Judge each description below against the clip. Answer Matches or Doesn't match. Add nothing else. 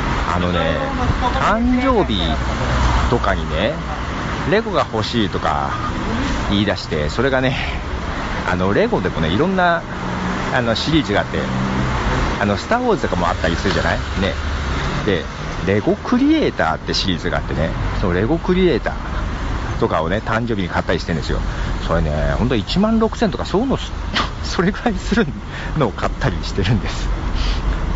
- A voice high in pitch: Doesn't match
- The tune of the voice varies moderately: Doesn't match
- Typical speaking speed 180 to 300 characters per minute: Doesn't match